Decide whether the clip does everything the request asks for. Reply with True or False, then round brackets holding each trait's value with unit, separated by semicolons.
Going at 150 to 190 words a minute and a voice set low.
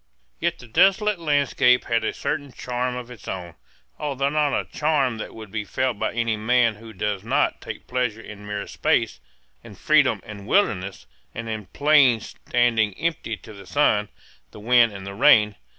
True (180 wpm; 115 Hz)